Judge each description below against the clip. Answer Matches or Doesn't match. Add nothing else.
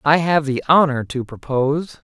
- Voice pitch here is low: Doesn't match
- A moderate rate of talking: Matches